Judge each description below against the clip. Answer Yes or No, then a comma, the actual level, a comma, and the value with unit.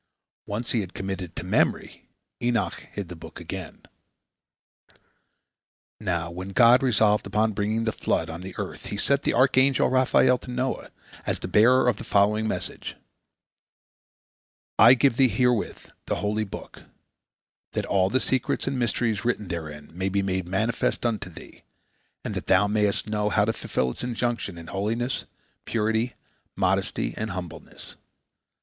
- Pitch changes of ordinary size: Yes, average, 3.9 semitones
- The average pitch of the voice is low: Yes, low, 105 Hz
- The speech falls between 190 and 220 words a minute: No, average, 155 wpm